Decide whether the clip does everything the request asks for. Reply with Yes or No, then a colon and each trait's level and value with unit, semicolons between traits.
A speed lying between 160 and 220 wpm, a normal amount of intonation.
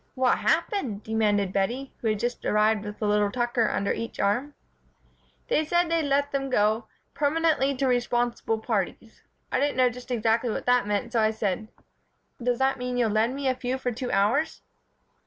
Yes: average, 190 wpm; average, 3.7 semitones